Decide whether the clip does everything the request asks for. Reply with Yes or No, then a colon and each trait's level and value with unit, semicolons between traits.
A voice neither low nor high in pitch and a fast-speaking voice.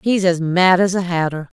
Yes: medium, 180 Hz; fast, 225 wpm